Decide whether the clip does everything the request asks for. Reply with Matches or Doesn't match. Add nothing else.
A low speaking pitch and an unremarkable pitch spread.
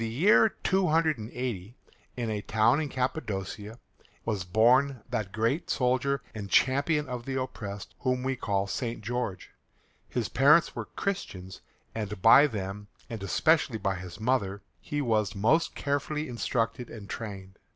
Matches